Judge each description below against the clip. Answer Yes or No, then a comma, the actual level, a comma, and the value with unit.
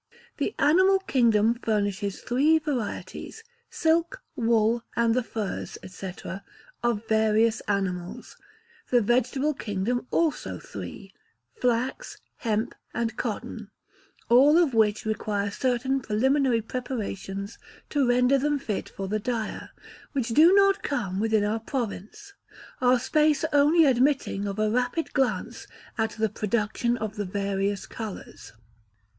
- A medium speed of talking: No, slow, 125 wpm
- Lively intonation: No, average, 4.3 semitones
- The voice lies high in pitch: Yes, high, 235 Hz